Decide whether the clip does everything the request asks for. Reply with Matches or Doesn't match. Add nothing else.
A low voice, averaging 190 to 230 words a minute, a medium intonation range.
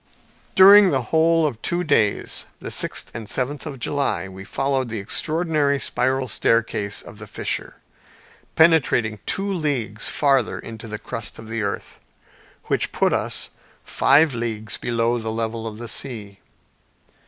Doesn't match